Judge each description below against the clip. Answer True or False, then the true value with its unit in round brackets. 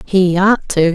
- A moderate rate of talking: True (190 wpm)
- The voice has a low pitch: False (185 Hz)